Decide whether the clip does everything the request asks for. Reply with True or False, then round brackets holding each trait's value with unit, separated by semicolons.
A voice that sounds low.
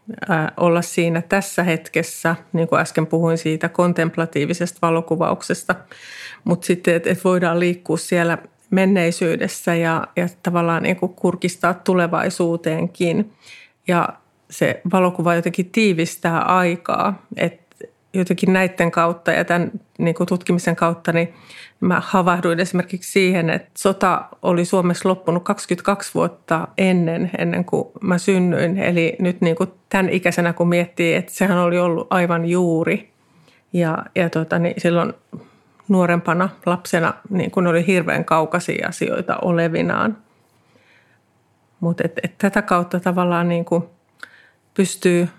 False (175 Hz)